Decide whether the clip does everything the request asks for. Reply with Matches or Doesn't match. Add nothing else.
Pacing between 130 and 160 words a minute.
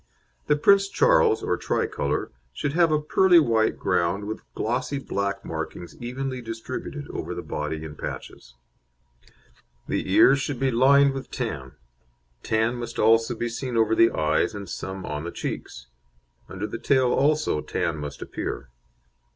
Matches